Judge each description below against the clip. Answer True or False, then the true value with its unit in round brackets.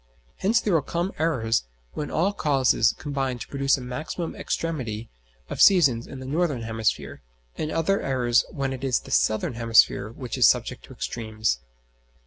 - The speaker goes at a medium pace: True (165 wpm)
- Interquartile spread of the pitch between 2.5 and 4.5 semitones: False (5.3 semitones)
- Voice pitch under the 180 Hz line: True (135 Hz)